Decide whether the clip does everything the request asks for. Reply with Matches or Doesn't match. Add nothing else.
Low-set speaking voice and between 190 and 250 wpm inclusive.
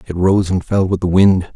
Doesn't match